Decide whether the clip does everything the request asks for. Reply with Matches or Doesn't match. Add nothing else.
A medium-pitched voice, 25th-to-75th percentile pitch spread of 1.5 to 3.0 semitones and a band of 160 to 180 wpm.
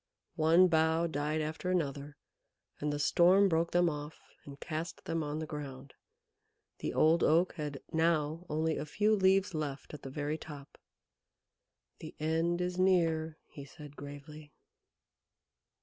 Doesn't match